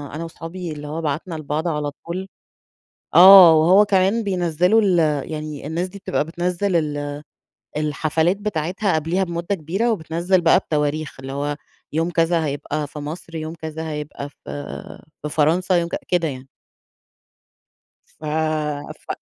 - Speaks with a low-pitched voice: No, medium, 165 Hz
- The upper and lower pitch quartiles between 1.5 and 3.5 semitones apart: Yes, average, 3.0 semitones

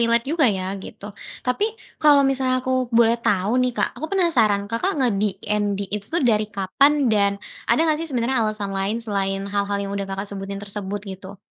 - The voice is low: No, high, 210 Hz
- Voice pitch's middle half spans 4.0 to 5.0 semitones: Yes, average, 4.4 semitones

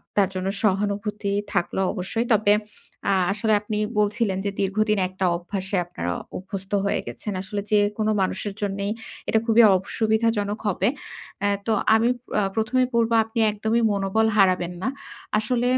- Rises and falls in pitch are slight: Yes, narrow, 2.1 semitones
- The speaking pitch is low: No, high, 205 Hz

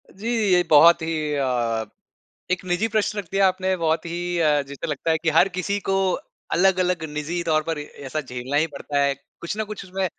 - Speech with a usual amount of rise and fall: Yes, average, 3.9 semitones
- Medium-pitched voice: Yes, medium, 165 Hz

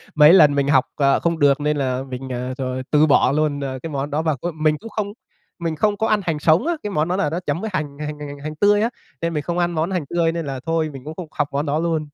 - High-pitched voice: No, medium, 155 Hz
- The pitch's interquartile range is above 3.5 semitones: No, average, 2.9 semitones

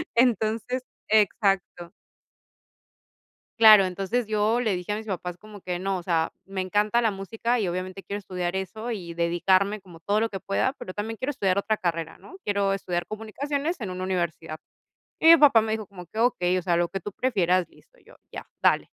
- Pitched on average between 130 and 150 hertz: No, high, 195 Hz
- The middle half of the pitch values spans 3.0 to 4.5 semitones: Yes, average, 3.5 semitones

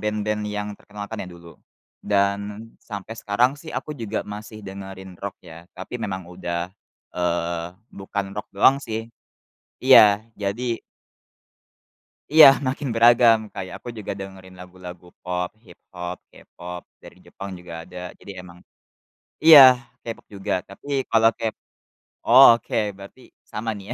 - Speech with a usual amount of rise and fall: Yes, average, 3.5 semitones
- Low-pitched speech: Yes, low, 100 Hz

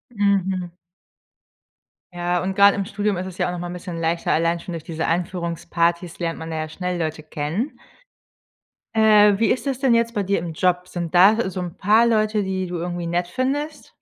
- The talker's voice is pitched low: No, medium, 180 Hz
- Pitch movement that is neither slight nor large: Yes, average, 3.3 semitones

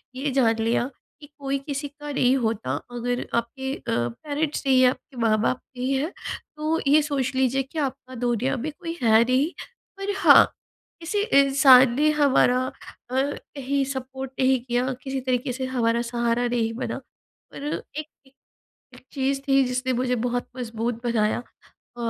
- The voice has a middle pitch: No, very high, 260 Hz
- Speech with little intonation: Yes, narrow, 2.3 semitones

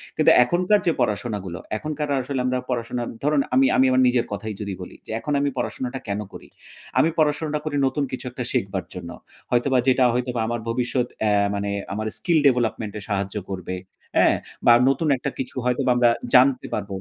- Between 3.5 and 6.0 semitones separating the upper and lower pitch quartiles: Yes, average, 4.3 semitones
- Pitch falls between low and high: No, low, 125 Hz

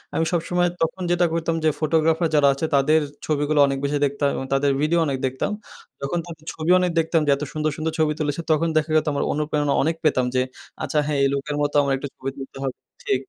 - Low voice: No, medium, 150 Hz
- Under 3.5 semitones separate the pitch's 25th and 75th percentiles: Yes, narrow, 2.5 semitones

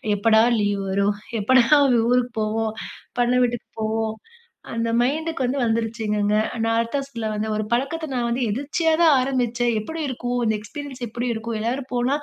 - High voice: Yes, high, 240 Hz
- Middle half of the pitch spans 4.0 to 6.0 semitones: No, average, 2.9 semitones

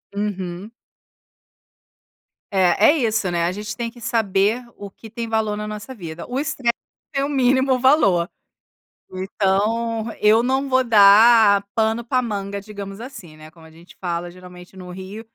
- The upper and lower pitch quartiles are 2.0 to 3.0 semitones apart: No, average, 3.8 semitones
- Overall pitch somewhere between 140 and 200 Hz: No, high, 210 Hz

